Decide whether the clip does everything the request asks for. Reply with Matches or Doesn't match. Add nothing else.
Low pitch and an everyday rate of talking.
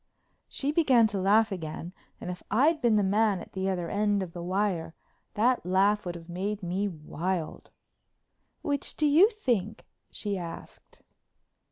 Doesn't match